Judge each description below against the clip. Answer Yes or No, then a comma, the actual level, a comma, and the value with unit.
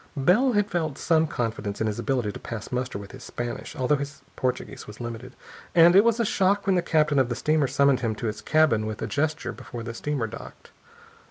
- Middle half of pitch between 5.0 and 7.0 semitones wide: Yes, wide, 5.5 semitones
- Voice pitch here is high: No, low, 135 Hz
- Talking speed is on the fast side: Yes, fast, 225 wpm